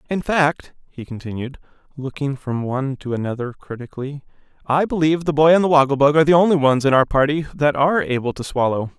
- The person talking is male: Yes, male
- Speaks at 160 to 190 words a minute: No, average, 200 wpm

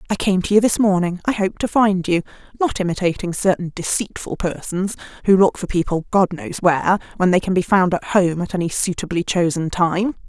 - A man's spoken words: No, female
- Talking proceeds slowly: No, fast, 205 wpm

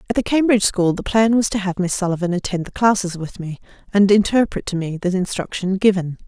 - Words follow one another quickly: Yes, fast, 220 wpm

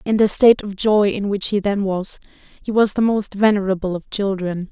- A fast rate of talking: Yes, fast, 215 wpm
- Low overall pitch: No, high, 200 Hz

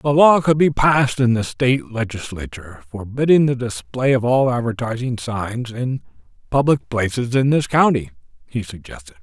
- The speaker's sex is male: Yes, male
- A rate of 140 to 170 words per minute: Yes, average, 155 wpm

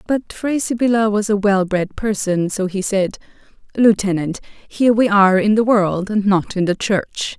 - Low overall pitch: No, high, 205 Hz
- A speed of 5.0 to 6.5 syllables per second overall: No, 4.7 syllables/s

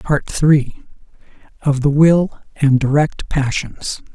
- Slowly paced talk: Yes, slow, 115 wpm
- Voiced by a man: Yes, male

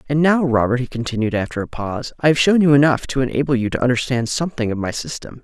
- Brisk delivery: Yes, fast, 245 wpm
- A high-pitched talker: No, low, 130 Hz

